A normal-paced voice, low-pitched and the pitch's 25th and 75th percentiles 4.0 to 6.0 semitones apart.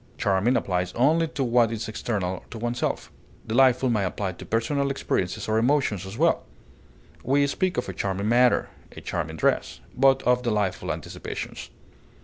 Yes: average, 155 wpm; low, 120 Hz; average, 4.7 semitones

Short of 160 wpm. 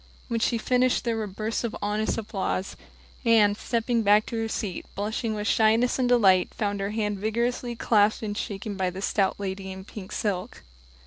No: average, 185 wpm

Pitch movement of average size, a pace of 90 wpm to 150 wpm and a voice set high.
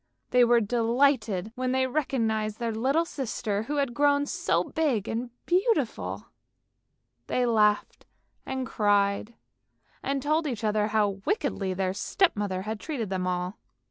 Yes: average, 4.8 semitones; average, 140 wpm; high, 230 Hz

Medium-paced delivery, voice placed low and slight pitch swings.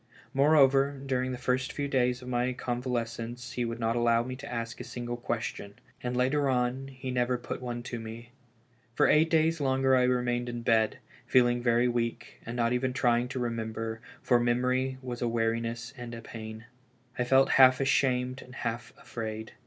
Yes: average, 185 wpm; low, 125 Hz; narrow, 1.6 semitones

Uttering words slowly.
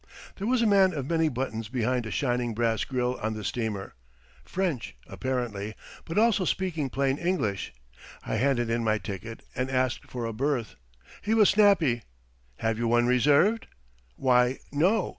No: average, 160 wpm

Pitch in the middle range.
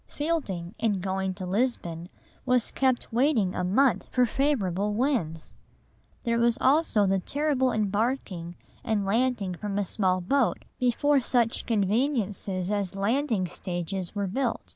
No: high, 210 Hz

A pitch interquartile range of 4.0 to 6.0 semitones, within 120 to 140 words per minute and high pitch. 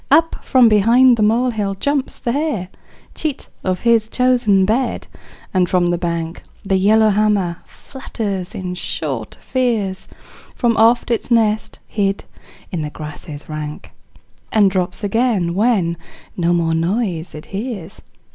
Yes: average, 4.9 semitones; slow, 135 wpm; high, 205 Hz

